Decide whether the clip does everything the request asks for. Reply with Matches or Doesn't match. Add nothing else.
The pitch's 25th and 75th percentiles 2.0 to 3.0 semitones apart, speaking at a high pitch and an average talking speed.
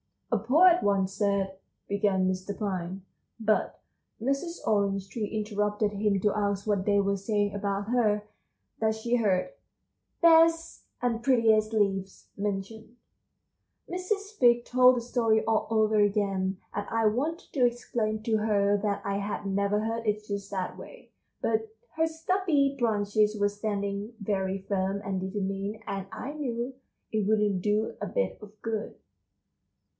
Matches